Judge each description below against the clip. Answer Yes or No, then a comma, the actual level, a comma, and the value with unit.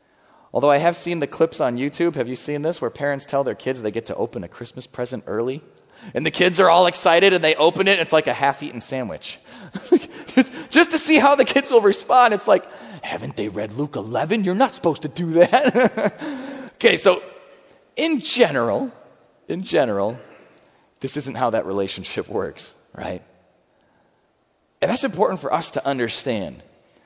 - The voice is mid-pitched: Yes, medium, 170 Hz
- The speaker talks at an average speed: Yes, average, 185 wpm